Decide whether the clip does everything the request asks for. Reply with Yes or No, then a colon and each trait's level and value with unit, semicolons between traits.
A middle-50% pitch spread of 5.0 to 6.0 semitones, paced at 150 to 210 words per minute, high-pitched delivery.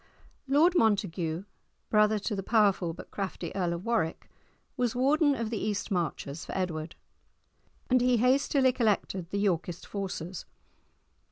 No: wide, 5.6 semitones; average, 140 wpm; high, 205 Hz